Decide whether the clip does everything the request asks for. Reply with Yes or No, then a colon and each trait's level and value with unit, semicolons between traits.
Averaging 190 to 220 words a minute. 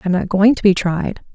No: fast, 270 wpm